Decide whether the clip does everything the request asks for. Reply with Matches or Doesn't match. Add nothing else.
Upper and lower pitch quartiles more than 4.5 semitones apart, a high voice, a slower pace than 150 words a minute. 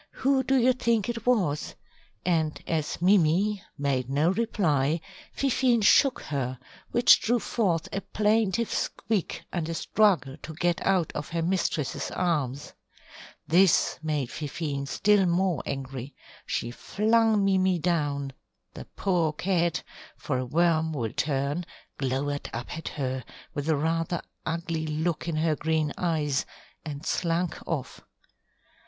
Doesn't match